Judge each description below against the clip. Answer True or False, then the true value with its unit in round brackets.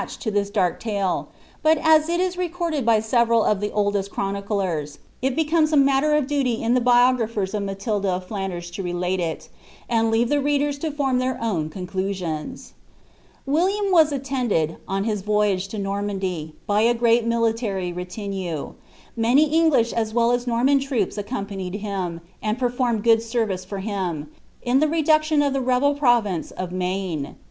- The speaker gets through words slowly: False (170 wpm)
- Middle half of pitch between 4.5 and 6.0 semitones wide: True (5.6 semitones)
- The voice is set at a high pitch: True (225 Hz)